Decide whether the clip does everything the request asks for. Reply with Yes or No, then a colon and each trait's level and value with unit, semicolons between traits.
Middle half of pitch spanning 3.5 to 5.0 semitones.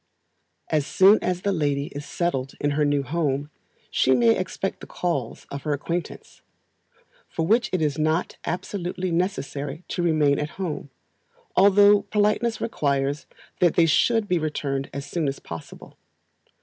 Yes: average, 4.5 semitones